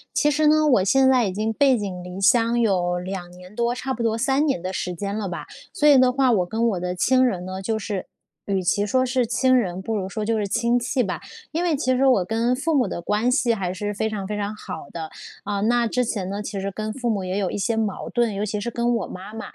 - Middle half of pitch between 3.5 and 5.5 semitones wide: Yes, average, 4.4 semitones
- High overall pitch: Yes, high, 220 Hz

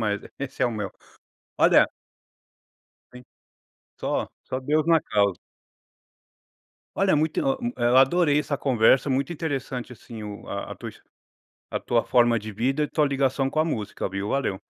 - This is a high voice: No, low, 130 Hz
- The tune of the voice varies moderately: Yes, average, 4.7 semitones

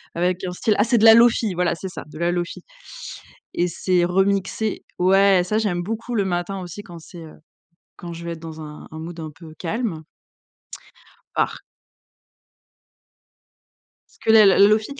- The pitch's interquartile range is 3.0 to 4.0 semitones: Yes, average, 3.3 semitones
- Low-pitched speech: No, medium, 180 Hz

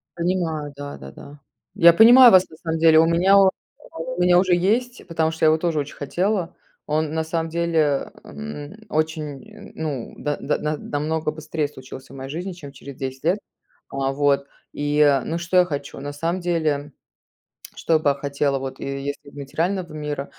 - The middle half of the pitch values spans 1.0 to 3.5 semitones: Yes, average, 3.1 semitones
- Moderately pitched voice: Yes, medium, 155 Hz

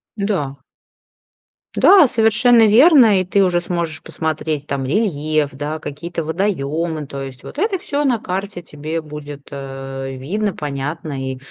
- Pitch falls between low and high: Yes, medium, 160 Hz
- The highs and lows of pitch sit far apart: Yes, wide, 6.2 semitones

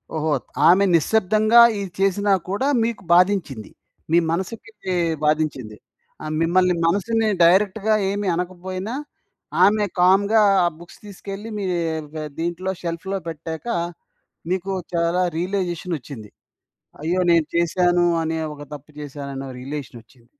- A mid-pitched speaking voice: Yes, medium, 180 Hz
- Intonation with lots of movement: No, average, 3.7 semitones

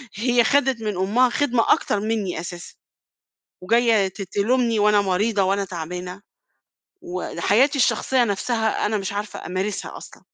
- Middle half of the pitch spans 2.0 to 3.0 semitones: No, average, 3.7 semitones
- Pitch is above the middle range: Yes, high, 210 Hz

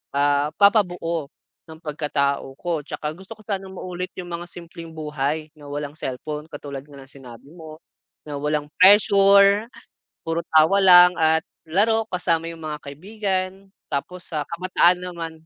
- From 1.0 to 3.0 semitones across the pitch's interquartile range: No, average, 3.6 semitones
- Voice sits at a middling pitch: Yes, medium, 165 Hz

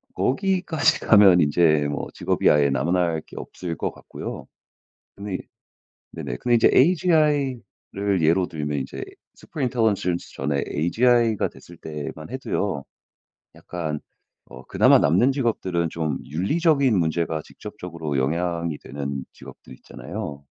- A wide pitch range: Yes, wide, 7.4 semitones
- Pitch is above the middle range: No, very low, 85 Hz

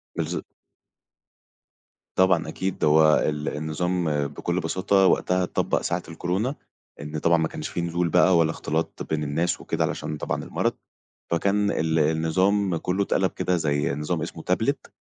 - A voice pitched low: Yes, very low, 85 Hz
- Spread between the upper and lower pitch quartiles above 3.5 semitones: No, average, 2.9 semitones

